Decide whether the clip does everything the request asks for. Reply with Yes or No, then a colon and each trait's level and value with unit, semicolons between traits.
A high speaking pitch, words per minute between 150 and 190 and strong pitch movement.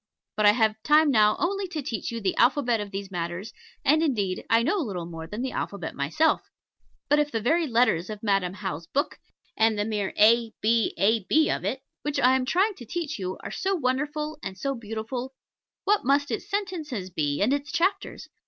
No: high, 235 Hz; average, 200 wpm; wide, 6.5 semitones